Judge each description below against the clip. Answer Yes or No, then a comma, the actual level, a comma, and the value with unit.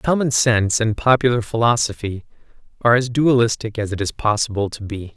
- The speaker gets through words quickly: No, average, 165 wpm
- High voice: No, low, 115 Hz